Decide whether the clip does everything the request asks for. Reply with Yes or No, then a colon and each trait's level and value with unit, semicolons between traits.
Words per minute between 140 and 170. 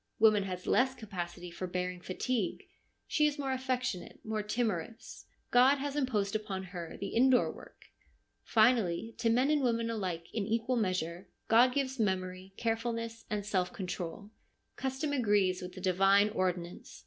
Yes: average, 150 wpm